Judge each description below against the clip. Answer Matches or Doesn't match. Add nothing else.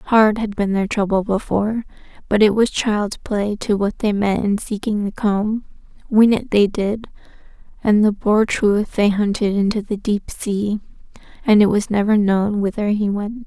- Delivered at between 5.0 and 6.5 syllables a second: Doesn't match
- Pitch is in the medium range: Doesn't match